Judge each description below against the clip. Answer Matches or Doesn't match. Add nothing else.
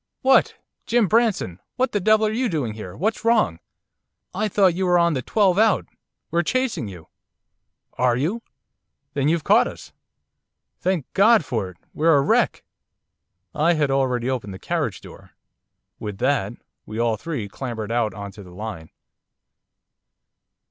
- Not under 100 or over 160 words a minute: Matches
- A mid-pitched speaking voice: Matches